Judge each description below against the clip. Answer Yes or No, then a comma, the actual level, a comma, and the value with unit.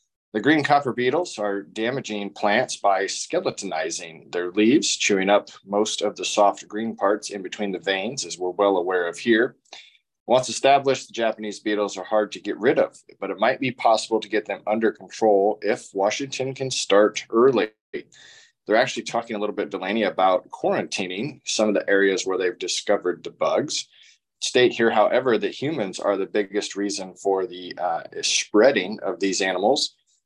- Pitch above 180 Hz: No, low, 105 Hz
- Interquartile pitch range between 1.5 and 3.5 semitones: Yes, average, 2.9 semitones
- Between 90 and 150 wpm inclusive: No, average, 175 wpm